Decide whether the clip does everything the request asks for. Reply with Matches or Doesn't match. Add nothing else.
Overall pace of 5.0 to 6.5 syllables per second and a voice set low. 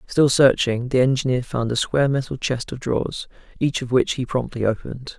Matches